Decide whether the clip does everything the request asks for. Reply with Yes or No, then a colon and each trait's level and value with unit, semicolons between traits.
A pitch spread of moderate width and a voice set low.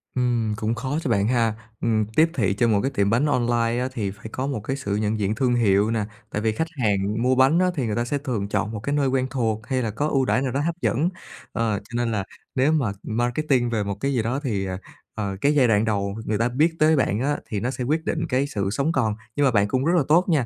Yes: average, 4.2 semitones; low, 120 Hz